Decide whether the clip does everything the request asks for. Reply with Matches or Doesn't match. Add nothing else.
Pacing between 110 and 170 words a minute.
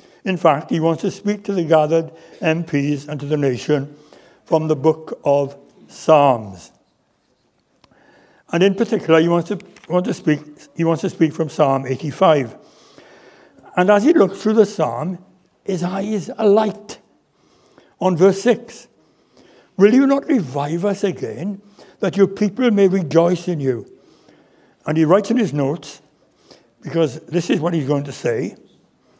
Matches